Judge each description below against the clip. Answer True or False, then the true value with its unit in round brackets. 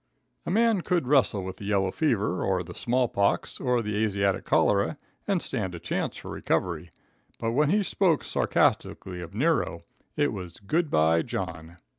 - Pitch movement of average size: False (8.1 semitones)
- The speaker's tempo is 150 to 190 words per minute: True (170 wpm)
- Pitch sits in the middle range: False (105 Hz)